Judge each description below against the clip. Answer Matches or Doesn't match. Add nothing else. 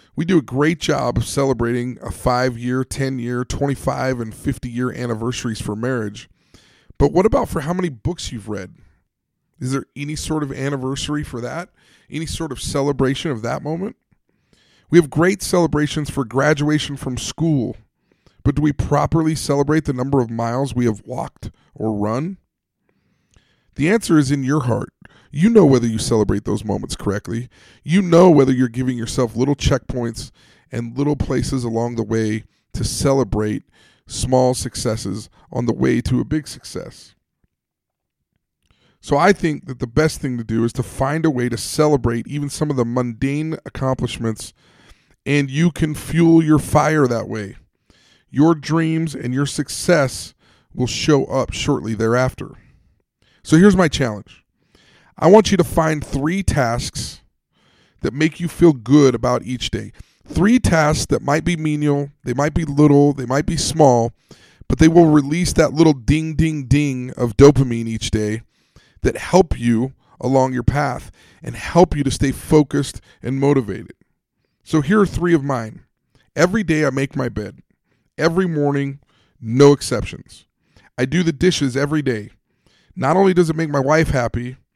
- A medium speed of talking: Matches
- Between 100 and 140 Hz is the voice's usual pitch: Matches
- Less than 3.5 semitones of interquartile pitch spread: Doesn't match